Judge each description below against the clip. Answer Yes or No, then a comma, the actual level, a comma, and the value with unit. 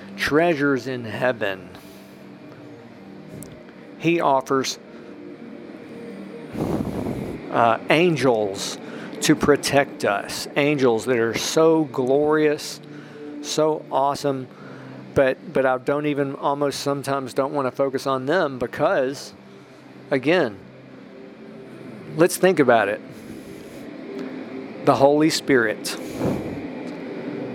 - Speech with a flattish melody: Yes, narrow, 2.2 semitones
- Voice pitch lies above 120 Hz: Yes, medium, 140 Hz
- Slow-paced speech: Yes, slow, 85 wpm